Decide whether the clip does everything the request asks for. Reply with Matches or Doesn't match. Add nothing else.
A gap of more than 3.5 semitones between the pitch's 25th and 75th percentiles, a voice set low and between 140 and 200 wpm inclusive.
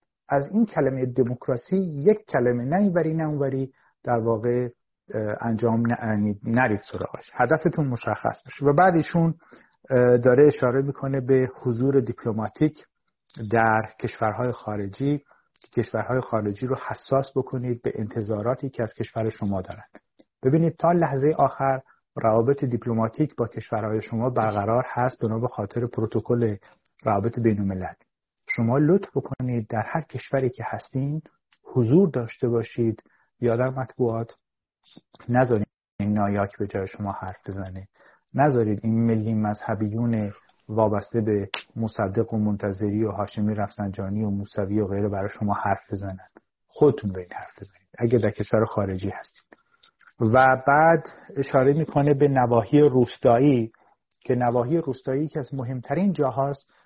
Doesn't match